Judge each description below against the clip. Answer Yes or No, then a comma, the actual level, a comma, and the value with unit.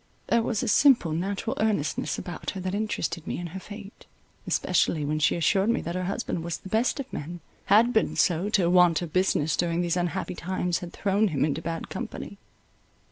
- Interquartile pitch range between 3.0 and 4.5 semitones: Yes, average, 3.6 semitones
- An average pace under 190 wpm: No, average, 195 wpm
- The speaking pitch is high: No, medium, 180 Hz